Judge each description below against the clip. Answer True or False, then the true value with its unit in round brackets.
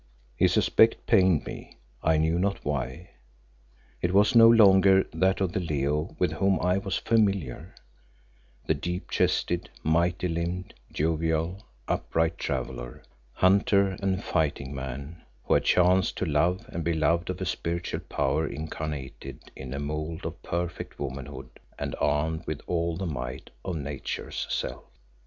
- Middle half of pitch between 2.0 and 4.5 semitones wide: True (3.9 semitones)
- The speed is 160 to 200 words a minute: False (145 wpm)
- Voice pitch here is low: True (85 Hz)